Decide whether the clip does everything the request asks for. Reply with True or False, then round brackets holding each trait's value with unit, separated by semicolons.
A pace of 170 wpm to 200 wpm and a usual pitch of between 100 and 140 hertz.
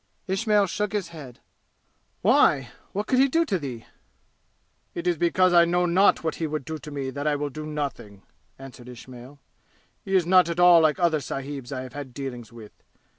False (195 wpm; 155 Hz)